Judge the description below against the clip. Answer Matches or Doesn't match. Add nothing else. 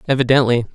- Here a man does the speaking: Matches